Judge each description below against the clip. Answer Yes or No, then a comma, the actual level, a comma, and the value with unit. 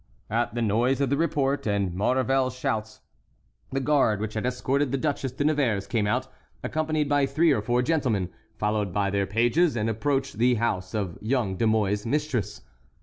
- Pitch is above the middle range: No, low, 120 Hz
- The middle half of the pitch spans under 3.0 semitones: No, average, 4.7 semitones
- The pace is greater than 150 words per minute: Yes, average, 180 wpm